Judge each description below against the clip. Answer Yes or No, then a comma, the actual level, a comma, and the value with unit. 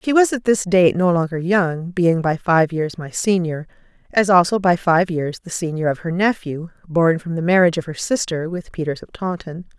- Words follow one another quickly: Yes, fast, 215 wpm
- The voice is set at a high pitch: No, medium, 175 Hz